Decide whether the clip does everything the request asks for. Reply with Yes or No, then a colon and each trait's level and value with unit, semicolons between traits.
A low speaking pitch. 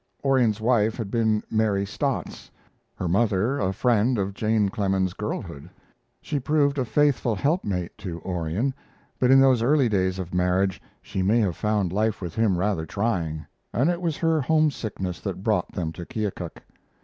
Yes: low, 105 Hz